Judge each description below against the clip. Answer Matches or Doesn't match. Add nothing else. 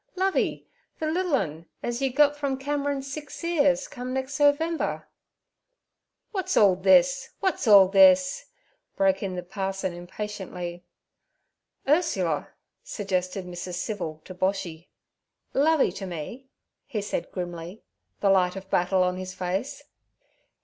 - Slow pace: Matches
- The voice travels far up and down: Matches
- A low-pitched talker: Doesn't match